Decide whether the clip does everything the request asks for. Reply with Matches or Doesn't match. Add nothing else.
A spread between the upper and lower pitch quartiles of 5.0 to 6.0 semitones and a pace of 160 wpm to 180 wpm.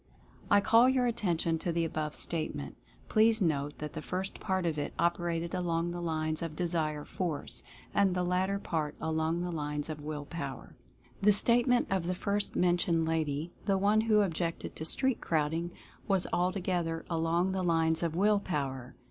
Doesn't match